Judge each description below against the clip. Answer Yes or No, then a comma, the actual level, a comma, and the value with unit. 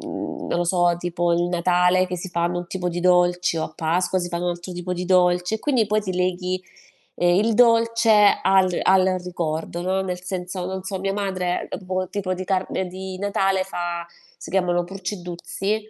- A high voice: No, medium, 180 Hz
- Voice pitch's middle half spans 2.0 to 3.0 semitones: No, narrow, 1.5 semitones